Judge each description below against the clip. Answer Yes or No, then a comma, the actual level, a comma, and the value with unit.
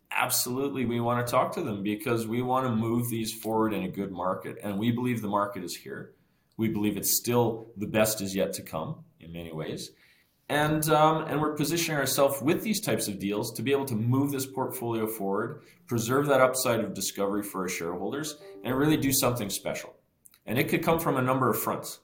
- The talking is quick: Yes, fast, 215 wpm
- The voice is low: Yes, low, 120 Hz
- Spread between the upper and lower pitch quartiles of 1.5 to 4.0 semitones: No, average, 4.8 semitones